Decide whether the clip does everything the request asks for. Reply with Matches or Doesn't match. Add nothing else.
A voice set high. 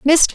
Matches